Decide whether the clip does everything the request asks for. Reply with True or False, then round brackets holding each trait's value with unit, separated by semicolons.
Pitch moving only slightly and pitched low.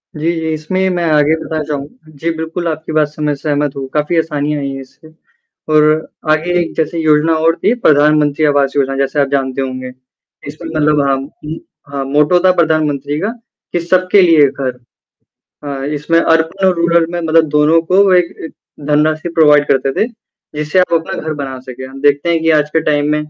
False (2.2 semitones; 150 Hz)